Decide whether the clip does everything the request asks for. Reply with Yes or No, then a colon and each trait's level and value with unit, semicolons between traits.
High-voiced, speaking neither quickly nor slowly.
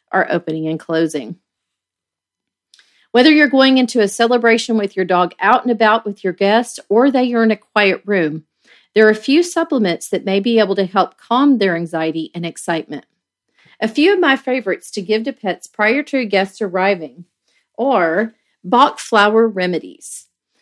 Yes: high, 210 Hz; average, 170 wpm